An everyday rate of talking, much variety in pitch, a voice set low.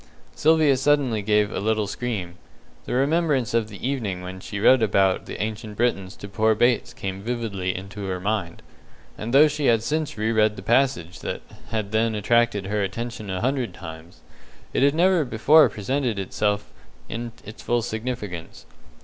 No: average, 175 wpm; average, 4.0 semitones; low, 110 Hz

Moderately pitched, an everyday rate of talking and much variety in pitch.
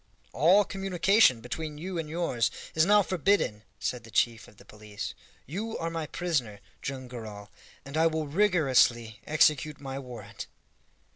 Yes: medium, 150 Hz; average, 150 wpm; wide, 6.5 semitones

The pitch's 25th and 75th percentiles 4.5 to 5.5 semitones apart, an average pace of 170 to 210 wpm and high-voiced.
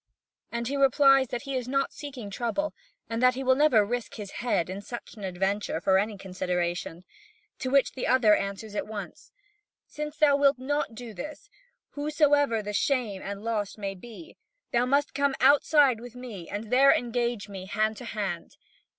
Yes: average, 5.1 semitones; average, 180 wpm; high, 235 Hz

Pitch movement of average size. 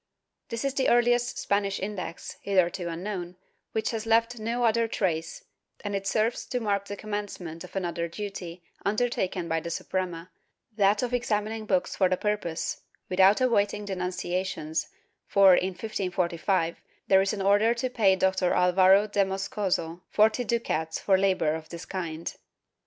Yes: average, 3.0 semitones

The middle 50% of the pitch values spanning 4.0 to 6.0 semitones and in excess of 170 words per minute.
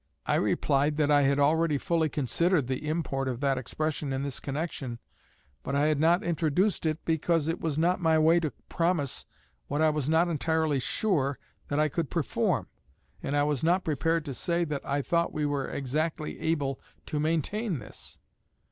No: average, 2.7 semitones; average, 185 wpm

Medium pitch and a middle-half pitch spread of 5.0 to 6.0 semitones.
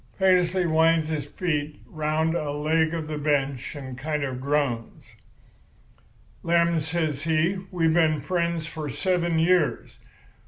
No: medium, 160 Hz; narrow, 2.4 semitones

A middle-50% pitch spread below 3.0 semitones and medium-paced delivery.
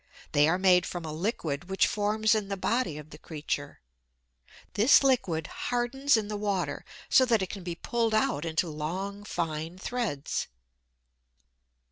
No: average, 5.3 semitones; average, 155 wpm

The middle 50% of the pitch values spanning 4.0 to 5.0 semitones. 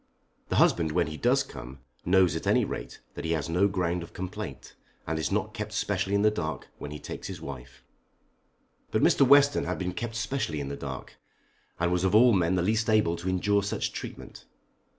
Yes: average, 4.5 semitones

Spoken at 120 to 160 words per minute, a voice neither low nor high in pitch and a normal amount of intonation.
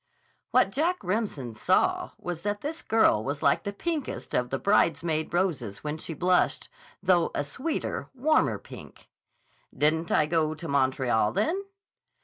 No: average, 145 wpm; medium, 170 Hz; wide, 7.1 semitones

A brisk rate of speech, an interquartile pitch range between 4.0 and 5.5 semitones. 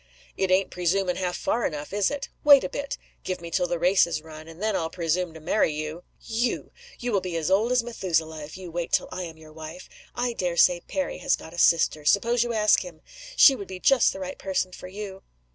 Yes: fast, 240 wpm; average, 4.5 semitones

